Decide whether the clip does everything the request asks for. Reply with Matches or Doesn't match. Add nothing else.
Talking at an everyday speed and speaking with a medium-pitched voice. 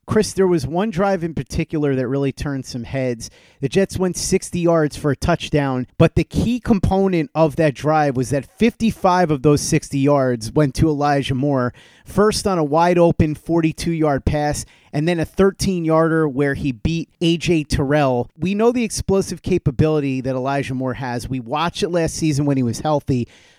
Matches